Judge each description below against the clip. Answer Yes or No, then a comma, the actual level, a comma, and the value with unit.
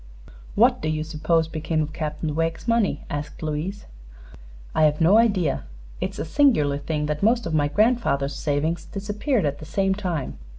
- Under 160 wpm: No, average, 170 wpm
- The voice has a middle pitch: Yes, medium, 160 Hz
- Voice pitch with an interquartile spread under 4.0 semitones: No, average, 4.6 semitones